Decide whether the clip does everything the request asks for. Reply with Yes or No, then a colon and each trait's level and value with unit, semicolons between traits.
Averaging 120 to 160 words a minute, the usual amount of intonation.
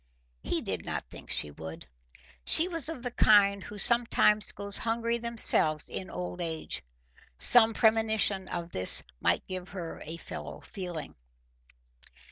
Yes: average, 140 wpm; average, 4.9 semitones